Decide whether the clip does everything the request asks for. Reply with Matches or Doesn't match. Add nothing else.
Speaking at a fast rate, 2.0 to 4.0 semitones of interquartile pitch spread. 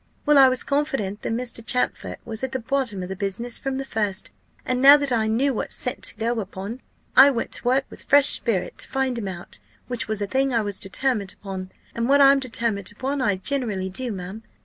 Doesn't match